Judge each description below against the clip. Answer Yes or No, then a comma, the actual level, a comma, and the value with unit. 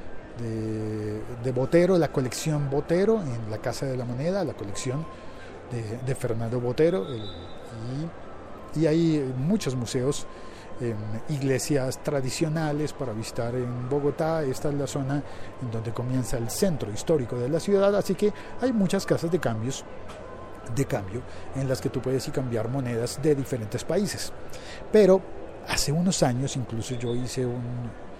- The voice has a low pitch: Yes, low, 130 Hz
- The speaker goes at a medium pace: Yes, average, 150 wpm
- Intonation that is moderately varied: Yes, average, 4.6 semitones